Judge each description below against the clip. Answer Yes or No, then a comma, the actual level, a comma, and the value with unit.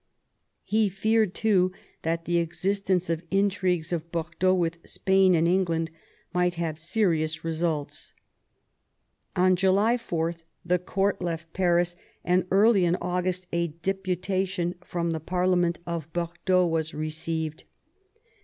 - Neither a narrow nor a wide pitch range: No, narrow, 2.1 semitones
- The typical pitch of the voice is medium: Yes, medium, 175 Hz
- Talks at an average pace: No, slow, 125 wpm